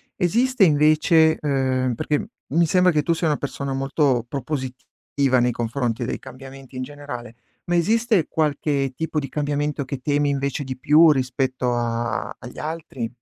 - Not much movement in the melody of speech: No, average, 3.2 semitones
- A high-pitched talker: No, medium, 140 Hz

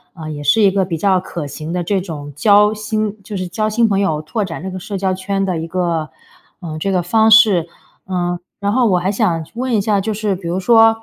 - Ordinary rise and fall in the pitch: Yes, average, 3.4 semitones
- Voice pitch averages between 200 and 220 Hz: No, high, 190 Hz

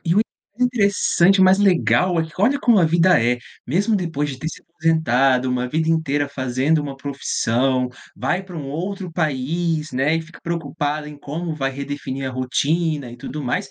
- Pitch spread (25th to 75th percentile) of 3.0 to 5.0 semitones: Yes, average, 4.3 semitones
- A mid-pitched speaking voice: Yes, medium, 155 Hz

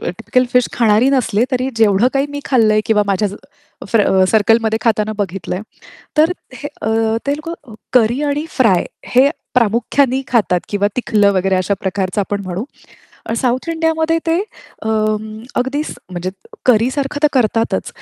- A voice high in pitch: Yes, high, 225 Hz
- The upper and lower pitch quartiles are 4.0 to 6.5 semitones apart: Yes, average, 4.5 semitones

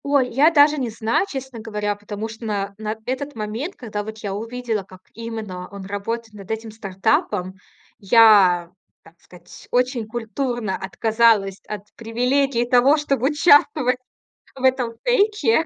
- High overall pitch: Yes, high, 225 Hz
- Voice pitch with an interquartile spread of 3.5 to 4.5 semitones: Yes, average, 3.9 semitones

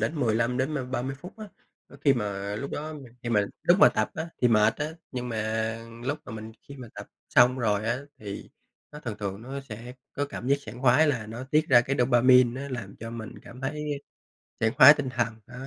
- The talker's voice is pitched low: Yes, low, 125 Hz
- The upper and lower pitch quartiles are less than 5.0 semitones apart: Yes, average, 3.7 semitones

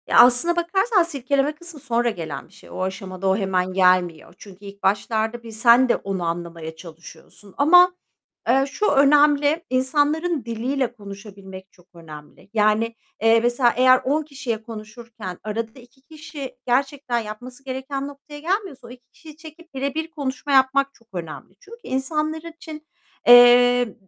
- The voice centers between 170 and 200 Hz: No, high, 245 Hz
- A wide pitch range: Yes, wide, 5.7 semitones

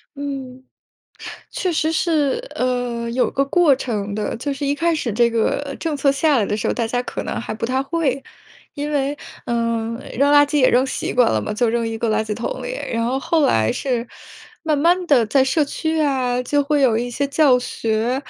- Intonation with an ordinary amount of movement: Yes, average, 3.8 semitones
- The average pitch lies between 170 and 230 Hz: No, very high, 265 Hz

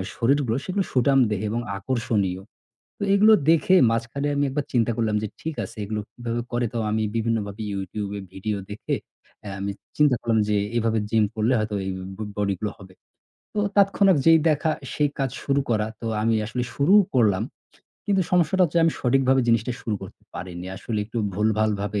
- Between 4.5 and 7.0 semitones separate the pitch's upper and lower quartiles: Yes, average, 4.9 semitones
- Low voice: Yes, low, 115 Hz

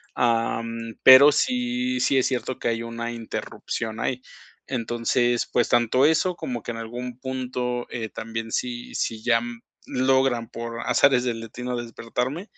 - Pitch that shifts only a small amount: Yes, narrow, 2.0 semitones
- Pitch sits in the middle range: No, low, 120 Hz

